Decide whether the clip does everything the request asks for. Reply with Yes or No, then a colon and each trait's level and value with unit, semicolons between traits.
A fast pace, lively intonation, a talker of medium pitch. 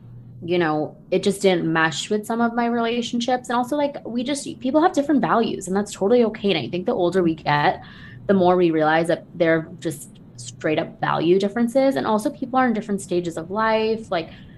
No: fast, 215 wpm; wide, 6.2 semitones; high, 195 Hz